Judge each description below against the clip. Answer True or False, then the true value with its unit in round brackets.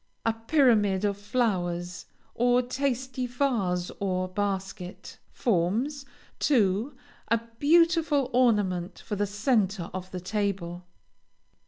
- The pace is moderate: False (105 wpm)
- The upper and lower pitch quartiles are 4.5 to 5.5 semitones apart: True (5.2 semitones)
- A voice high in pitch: True (210 Hz)